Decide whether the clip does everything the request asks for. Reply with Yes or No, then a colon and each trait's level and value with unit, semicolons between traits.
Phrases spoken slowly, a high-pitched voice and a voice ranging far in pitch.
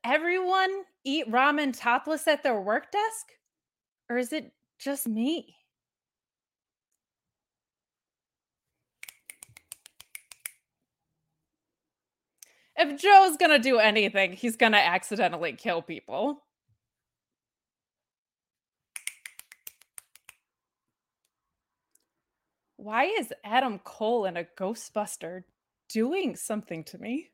Yes: slow, 75 wpm; very high, 250 Hz; wide, 6.6 semitones